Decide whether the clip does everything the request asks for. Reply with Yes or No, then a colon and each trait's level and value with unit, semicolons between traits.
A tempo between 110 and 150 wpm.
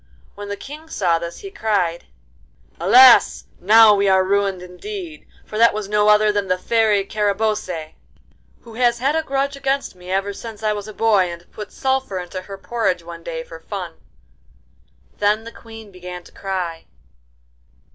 No: average, 170 wpm